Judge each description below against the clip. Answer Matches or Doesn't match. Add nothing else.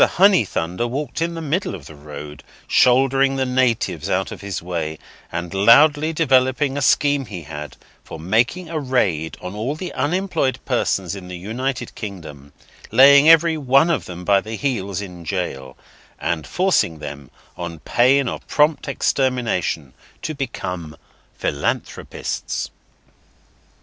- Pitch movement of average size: Doesn't match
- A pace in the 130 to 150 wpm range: Matches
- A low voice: Matches